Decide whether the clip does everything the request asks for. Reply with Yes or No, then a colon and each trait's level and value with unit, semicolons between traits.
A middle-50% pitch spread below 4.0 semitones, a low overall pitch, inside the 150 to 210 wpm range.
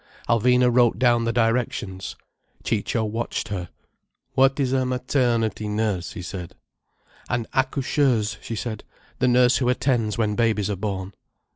No: average, 3.1 semitones; low, 115 Hz; average, 140 wpm